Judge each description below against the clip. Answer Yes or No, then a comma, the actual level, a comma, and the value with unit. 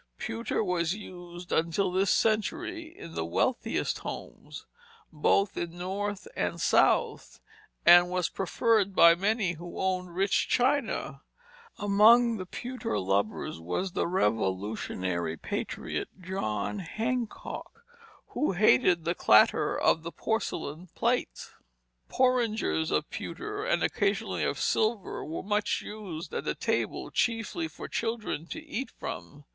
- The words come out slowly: Yes, slow, 125 wpm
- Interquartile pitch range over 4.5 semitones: Yes, average, 5.1 semitones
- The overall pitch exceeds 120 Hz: Yes, high, 190 Hz